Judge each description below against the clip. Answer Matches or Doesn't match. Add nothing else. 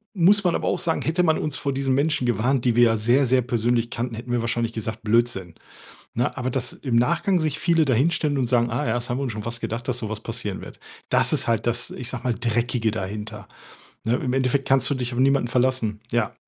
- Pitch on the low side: Matches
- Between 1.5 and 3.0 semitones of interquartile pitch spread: Matches